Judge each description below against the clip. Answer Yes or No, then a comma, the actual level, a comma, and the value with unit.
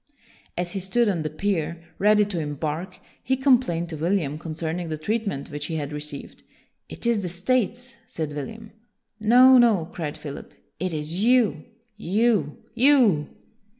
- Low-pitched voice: No, medium, 180 Hz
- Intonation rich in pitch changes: Yes, wide, 6.3 semitones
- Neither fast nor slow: Yes, average, 160 wpm